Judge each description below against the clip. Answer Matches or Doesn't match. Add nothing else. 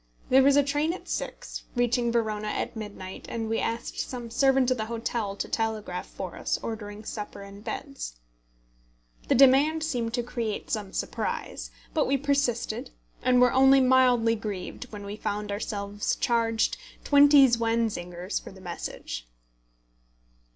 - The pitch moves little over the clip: Doesn't match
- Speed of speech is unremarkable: Matches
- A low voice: Doesn't match